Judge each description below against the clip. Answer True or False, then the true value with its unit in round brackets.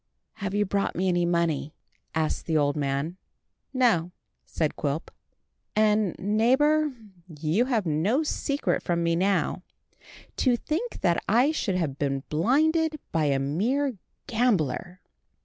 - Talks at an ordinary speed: False (130 wpm)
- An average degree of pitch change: False (7.6 semitones)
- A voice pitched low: False (185 Hz)